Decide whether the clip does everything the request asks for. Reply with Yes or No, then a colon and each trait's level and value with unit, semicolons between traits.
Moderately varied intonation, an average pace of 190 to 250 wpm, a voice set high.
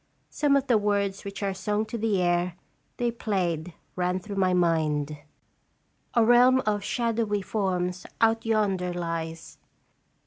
No: average, 3.9 semitones; average, 140 wpm; high, 200 Hz